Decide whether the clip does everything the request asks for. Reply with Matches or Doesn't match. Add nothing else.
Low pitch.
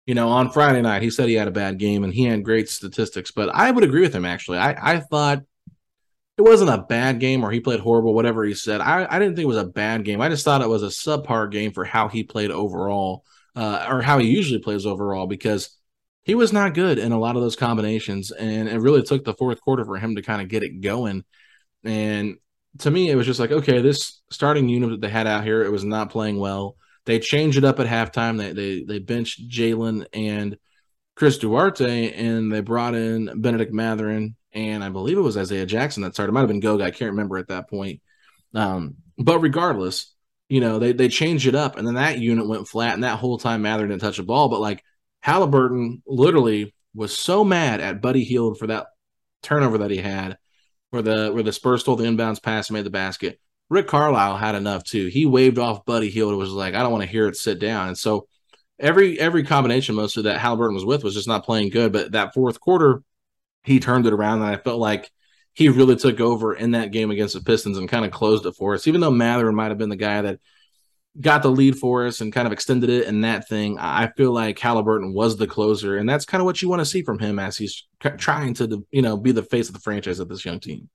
Matches